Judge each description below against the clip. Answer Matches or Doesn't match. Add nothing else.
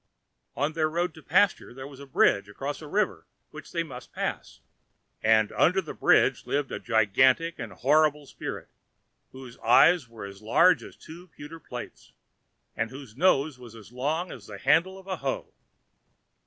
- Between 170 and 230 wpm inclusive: Matches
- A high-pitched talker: Doesn't match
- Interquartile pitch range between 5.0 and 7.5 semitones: Matches